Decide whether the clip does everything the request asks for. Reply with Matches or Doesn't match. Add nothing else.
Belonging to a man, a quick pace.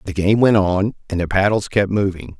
Matches